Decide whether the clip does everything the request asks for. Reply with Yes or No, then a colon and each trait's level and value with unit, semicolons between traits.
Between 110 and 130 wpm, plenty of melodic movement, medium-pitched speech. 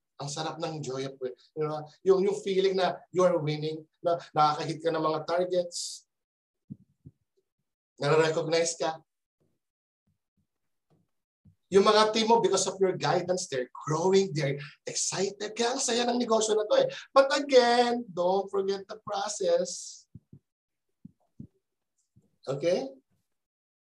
No: average, 125 wpm; average, 4.9 semitones; medium, 180 Hz